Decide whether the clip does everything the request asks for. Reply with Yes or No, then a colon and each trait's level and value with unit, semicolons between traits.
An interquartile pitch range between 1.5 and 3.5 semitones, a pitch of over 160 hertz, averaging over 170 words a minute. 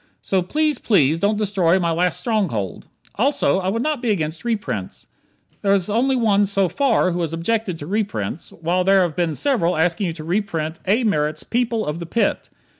No: average, 4.8 semitones; high, 190 Hz; average, 190 wpm